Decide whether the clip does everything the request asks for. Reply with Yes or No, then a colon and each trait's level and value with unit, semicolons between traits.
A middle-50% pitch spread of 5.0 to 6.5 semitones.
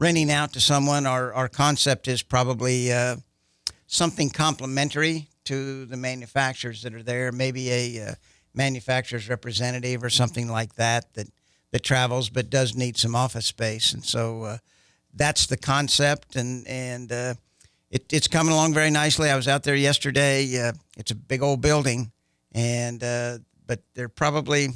No: average, 2.7 semitones